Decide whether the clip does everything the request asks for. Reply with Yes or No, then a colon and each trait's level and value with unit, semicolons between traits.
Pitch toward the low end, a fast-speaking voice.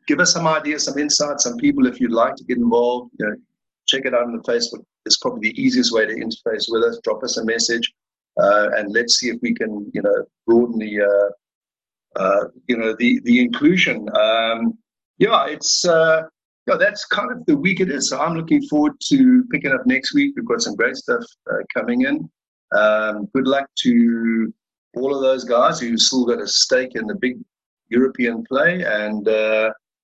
No: medium, 160 Hz; fast, 210 wpm